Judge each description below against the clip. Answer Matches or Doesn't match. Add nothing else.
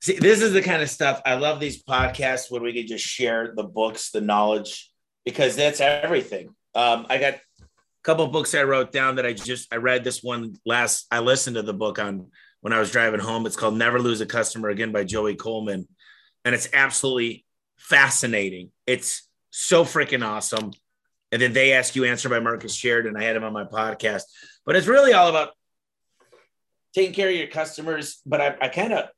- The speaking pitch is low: Matches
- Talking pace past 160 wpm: Matches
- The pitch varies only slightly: Doesn't match